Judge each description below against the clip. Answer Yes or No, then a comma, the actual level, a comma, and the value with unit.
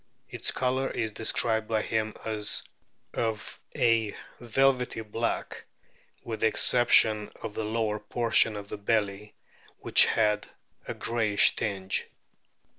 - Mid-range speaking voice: No, low, 110 Hz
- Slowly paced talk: Yes, slow, 120 wpm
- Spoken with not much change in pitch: Yes, narrow, 1.5 semitones